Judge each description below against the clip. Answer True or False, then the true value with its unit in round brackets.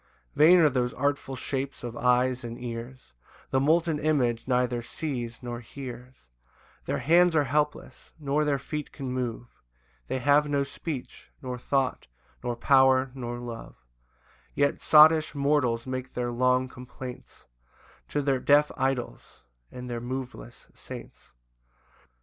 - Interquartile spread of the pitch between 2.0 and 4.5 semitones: True (2.7 semitones)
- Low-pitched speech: True (130 Hz)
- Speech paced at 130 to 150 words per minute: True (140 wpm)